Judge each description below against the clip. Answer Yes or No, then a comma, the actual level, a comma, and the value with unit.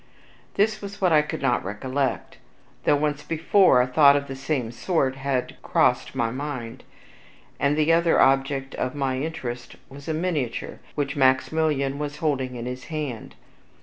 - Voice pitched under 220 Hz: Yes, medium, 140 Hz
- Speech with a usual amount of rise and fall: Yes, average, 3.0 semitones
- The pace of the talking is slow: No, average, 155 wpm